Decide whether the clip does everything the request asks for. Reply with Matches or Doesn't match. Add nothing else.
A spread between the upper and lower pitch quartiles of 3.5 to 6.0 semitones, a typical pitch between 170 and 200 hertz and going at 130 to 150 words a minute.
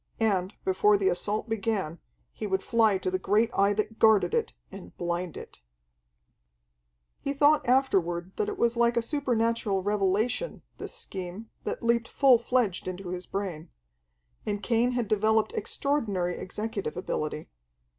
Doesn't match